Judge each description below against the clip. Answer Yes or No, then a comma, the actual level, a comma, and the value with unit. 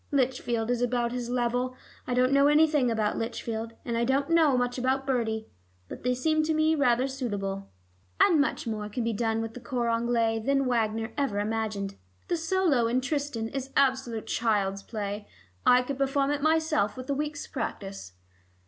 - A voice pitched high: Yes, high, 245 Hz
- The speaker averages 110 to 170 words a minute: No, average, 180 wpm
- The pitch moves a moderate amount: Yes, average, 3.6 semitones